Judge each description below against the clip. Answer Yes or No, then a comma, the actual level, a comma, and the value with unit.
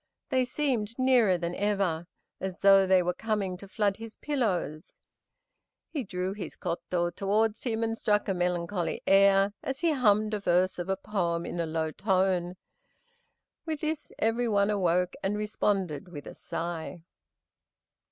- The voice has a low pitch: No, high, 195 Hz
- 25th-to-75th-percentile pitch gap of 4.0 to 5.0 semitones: No, average, 3.6 semitones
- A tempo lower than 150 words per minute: No, average, 155 wpm